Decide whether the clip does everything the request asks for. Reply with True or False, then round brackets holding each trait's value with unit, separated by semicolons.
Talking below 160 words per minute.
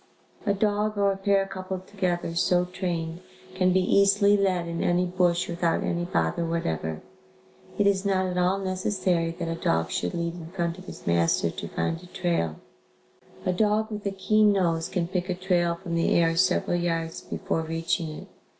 False (185 wpm)